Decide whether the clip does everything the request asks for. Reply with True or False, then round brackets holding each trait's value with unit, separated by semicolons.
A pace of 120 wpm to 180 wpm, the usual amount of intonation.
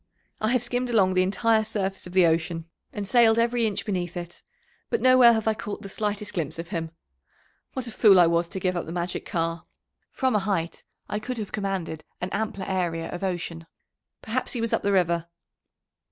False (205 wpm; 4.3 semitones)